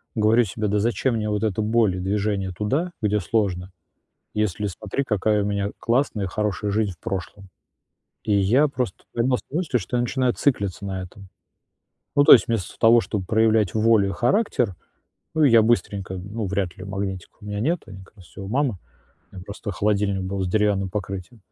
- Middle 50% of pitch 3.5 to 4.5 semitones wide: No, average, 2.9 semitones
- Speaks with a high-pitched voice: No, low, 105 Hz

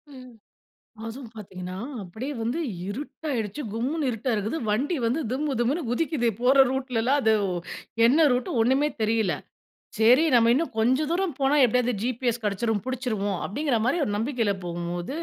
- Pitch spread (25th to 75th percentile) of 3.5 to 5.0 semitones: Yes, average, 3.8 semitones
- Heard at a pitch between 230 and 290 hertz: Yes, high, 245 Hz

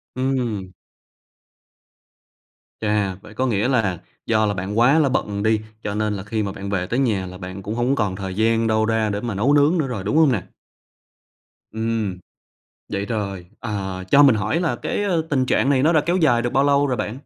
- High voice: No, low, 110 Hz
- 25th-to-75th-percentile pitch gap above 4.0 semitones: Yes, average, 4.6 semitones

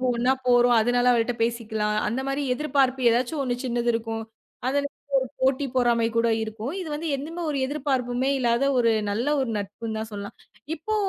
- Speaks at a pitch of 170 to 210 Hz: No, high, 245 Hz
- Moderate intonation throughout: Yes, average, 3.0 semitones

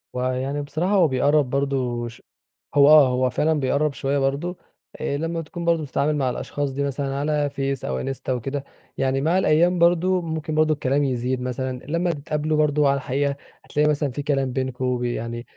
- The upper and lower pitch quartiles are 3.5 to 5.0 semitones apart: No, average, 2.8 semitones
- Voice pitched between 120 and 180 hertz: Yes, medium, 140 Hz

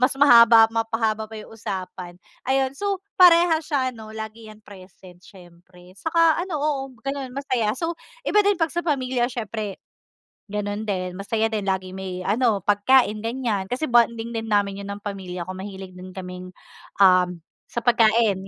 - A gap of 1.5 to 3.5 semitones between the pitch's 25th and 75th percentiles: No, average, 5.1 semitones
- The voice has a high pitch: Yes, high, 220 Hz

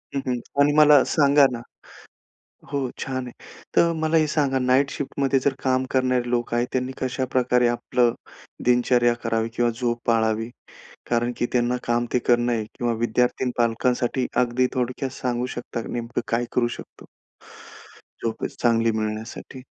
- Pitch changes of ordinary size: No, narrow, 1.7 semitones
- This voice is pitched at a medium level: No, low, 125 Hz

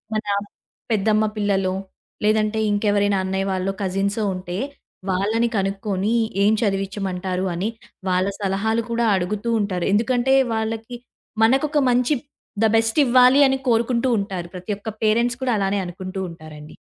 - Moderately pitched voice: No, high, 205 Hz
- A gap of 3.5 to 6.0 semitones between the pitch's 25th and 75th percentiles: No, average, 2.9 semitones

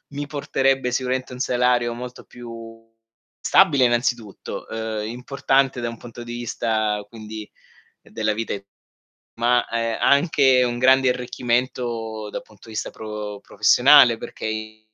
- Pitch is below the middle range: Yes, low, 120 Hz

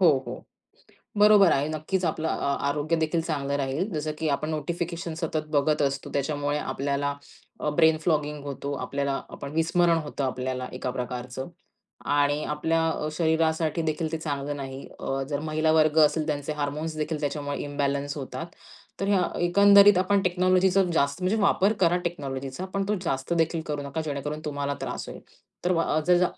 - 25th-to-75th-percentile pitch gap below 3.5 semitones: Yes, average, 2.8 semitones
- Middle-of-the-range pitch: Yes, medium, 155 Hz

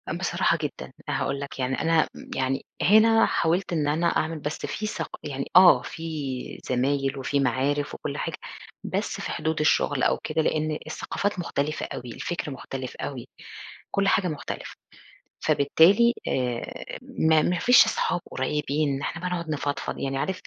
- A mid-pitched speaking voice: Yes, medium, 150 Hz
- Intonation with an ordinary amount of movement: Yes, average, 4.0 semitones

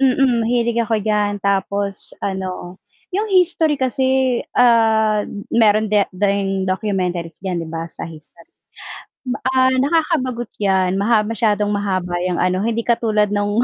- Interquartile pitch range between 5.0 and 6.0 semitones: No, average, 3.8 semitones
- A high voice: Yes, high, 210 Hz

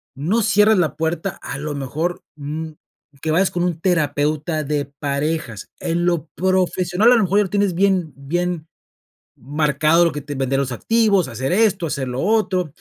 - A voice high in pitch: No, medium, 165 Hz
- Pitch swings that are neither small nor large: Yes, average, 4.2 semitones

